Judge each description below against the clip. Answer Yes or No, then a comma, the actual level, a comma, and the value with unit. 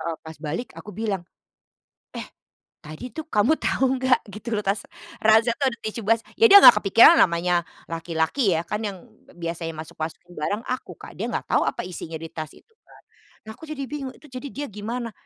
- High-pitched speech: Yes, high, 210 Hz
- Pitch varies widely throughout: Yes, wide, 7.1 semitones